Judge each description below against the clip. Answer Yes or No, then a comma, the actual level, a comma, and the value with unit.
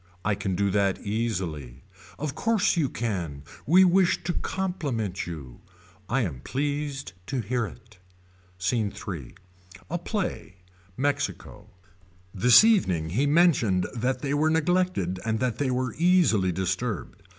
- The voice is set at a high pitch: No, low, 120 Hz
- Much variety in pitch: Yes, wide, 8.4 semitones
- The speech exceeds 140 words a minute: No, slow, 135 wpm